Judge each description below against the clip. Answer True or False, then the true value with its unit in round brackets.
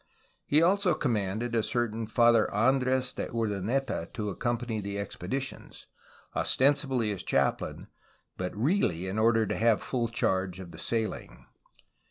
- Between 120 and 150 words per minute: True (140 wpm)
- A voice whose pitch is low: True (115 Hz)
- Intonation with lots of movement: False (4.1 semitones)